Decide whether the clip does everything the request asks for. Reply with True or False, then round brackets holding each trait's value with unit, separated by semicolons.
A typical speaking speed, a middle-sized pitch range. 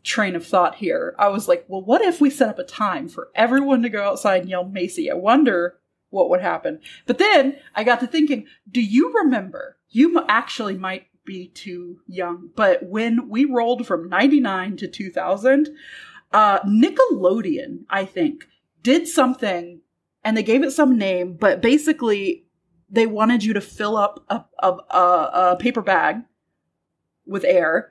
False (170 wpm; 6.3 semitones)